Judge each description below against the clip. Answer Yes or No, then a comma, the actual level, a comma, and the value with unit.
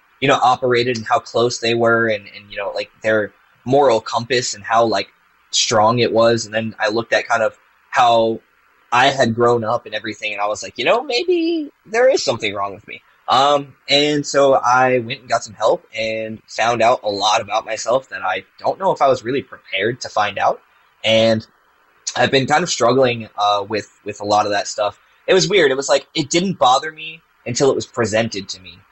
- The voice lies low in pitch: Yes, low, 115 Hz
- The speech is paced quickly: Yes, fast, 220 wpm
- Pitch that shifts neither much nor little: Yes, average, 4.1 semitones